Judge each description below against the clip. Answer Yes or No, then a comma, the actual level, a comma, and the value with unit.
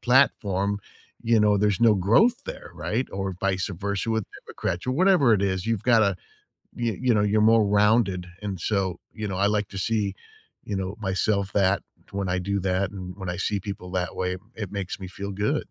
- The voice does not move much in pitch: Yes, narrow, 2.3 semitones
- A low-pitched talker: Yes, low, 100 Hz